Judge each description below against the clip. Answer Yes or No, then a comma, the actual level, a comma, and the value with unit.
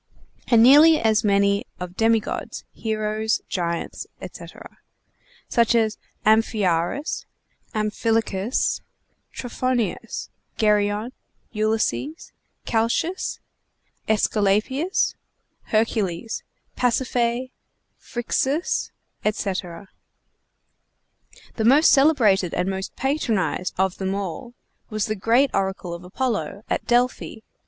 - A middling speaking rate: No, slow, 85 wpm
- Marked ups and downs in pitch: No, average, 3.6 semitones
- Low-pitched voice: No, high, 220 Hz